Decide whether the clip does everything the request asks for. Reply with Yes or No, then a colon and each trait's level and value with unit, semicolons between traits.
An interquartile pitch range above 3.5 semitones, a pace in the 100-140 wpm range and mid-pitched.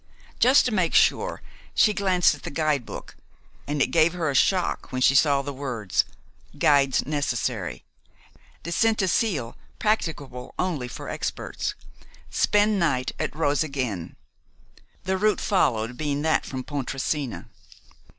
Yes: wide, 5.6 semitones; slow, 135 wpm; medium, 145 Hz